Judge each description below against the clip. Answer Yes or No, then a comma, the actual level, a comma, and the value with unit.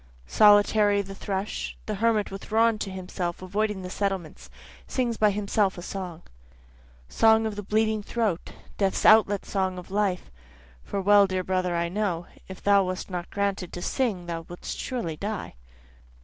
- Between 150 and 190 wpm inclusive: Yes, average, 160 wpm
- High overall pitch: Yes, high, 200 Hz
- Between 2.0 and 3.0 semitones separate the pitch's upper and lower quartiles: Yes, narrow, 2.5 semitones